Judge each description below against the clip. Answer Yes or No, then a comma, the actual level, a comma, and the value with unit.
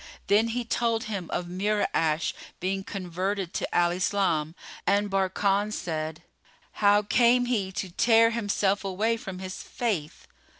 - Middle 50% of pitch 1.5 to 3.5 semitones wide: Yes, average, 2.9 semitones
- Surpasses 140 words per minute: No, slow, 135 wpm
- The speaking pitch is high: Yes, high, 195 Hz